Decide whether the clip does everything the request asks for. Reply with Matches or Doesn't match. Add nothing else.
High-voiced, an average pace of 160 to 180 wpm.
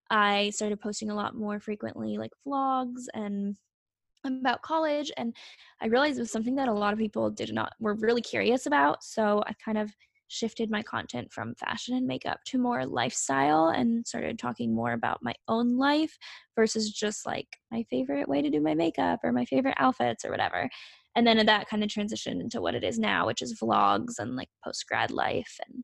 Doesn't match